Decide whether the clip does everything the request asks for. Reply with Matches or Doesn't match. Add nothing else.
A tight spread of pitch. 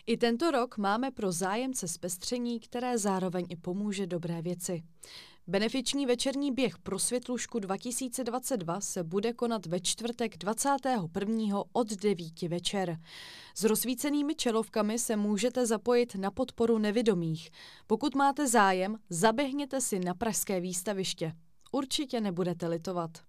Doesn't match